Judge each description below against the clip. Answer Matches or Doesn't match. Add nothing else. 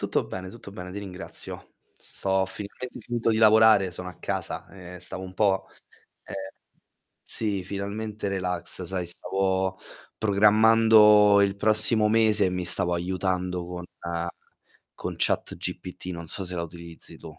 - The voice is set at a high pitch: Doesn't match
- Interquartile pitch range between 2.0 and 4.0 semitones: Matches